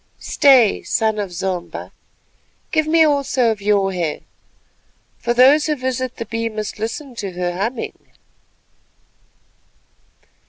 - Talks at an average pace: No, slow, 115 wpm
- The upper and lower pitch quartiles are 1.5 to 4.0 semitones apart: No, average, 4.6 semitones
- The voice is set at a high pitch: Yes, high, 230 Hz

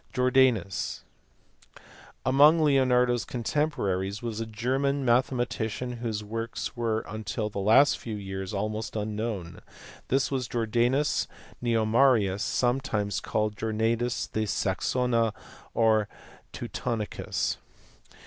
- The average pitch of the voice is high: No, low, 115 Hz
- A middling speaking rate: No, slow, 100 wpm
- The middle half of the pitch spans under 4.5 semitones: Yes, average, 2.8 semitones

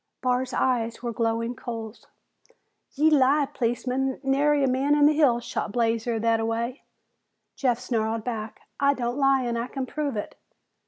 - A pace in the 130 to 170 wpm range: Yes, average, 155 wpm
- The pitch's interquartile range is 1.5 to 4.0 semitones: Yes, average, 2.8 semitones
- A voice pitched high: Yes, very high, 250 Hz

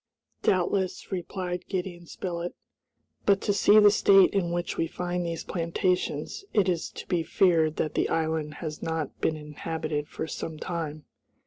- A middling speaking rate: Yes, average, 155 wpm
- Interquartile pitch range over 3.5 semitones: No, narrow, 2.5 semitones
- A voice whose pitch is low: No, medium, 170 Hz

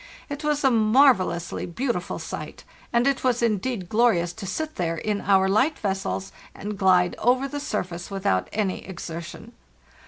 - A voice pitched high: Yes, high, 205 Hz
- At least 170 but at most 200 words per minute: No, average, 155 wpm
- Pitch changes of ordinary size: No, wide, 6.0 semitones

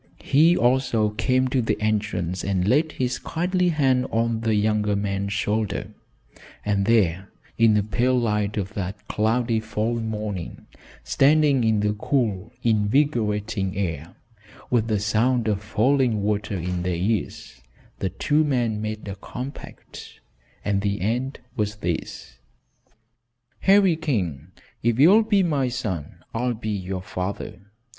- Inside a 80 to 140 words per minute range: Yes, slow, 135 wpm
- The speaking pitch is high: No, low, 110 Hz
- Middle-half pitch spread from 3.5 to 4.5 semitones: Yes, average, 3.8 semitones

